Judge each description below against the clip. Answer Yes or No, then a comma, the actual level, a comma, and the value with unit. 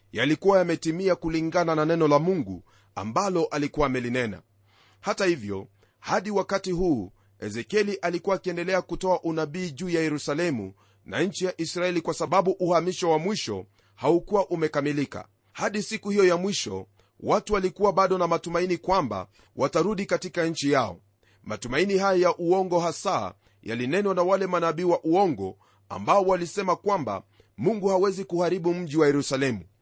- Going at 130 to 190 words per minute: Yes, fast, 140 wpm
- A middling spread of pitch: No, wide, 8.3 semitones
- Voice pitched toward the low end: No, medium, 165 Hz